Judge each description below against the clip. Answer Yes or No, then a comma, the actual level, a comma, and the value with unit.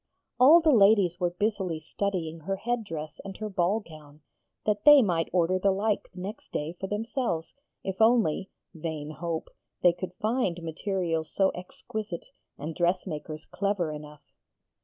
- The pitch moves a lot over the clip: No, average, 4.1 semitones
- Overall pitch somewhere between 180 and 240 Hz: Yes, medium, 185 Hz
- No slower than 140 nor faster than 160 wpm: Yes, average, 150 wpm